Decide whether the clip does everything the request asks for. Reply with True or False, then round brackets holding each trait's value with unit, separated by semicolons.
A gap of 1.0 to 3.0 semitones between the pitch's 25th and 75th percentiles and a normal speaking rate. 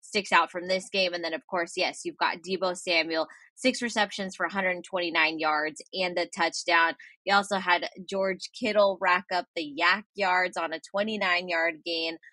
True (2.6 semitones; 180 wpm)